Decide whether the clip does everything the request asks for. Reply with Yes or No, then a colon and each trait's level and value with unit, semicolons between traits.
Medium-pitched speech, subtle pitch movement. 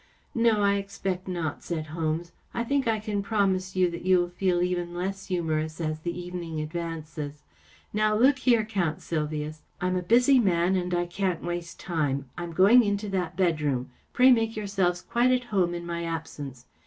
No: medium, 180 Hz; average, 3.7 semitones